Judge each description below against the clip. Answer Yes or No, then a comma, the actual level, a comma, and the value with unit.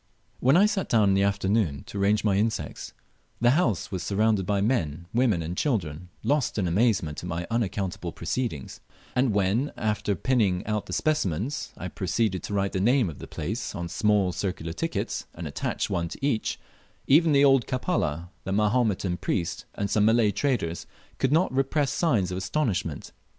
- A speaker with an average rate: Yes, average, 175 wpm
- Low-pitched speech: Yes, low, 105 Hz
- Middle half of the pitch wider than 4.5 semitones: Yes, wide, 5.4 semitones